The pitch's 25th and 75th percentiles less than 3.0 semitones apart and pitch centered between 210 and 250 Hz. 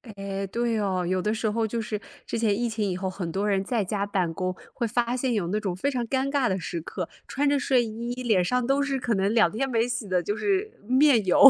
No: average, 4.2 semitones; high, 220 Hz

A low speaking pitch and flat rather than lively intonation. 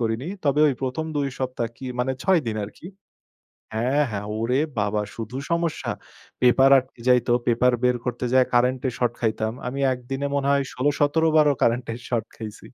No: low, 125 Hz; average, 3.2 semitones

